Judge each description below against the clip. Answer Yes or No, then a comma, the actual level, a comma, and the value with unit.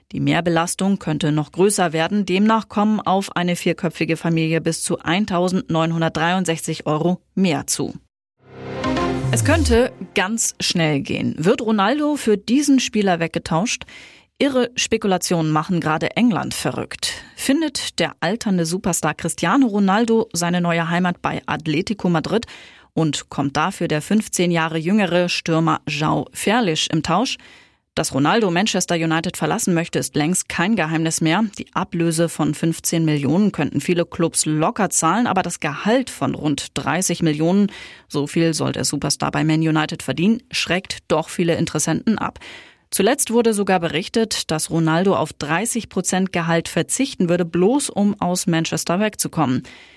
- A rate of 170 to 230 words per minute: No, average, 140 wpm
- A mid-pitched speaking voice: Yes, medium, 175 Hz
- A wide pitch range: No, average, 4.1 semitones